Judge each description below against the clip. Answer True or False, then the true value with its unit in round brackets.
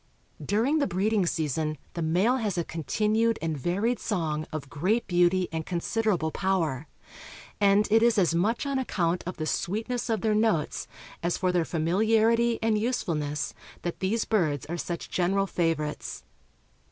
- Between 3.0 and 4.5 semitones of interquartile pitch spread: False (5.1 semitones)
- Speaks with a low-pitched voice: False (185 Hz)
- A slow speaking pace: False (155 wpm)